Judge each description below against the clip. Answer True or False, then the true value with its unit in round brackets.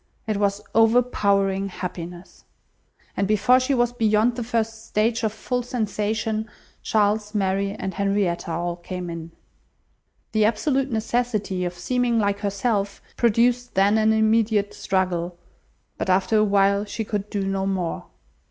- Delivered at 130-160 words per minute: True (140 wpm)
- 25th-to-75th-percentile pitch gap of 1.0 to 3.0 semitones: True (2.6 semitones)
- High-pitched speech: True (210 Hz)